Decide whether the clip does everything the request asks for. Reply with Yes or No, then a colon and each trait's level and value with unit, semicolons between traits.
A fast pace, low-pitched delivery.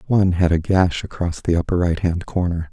Yes: fast, 220 wpm; very low, 90 Hz